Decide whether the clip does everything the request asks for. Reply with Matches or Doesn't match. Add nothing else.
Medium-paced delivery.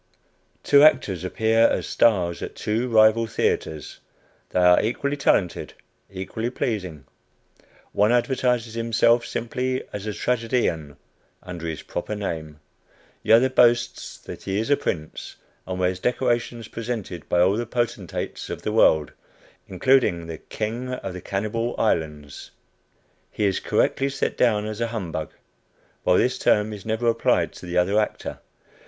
Matches